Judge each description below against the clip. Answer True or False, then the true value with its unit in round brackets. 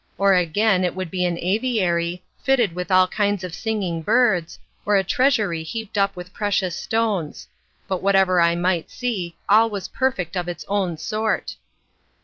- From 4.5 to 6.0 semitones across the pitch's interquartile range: False (3.4 semitones)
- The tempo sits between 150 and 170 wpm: True (165 wpm)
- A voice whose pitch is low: False (190 Hz)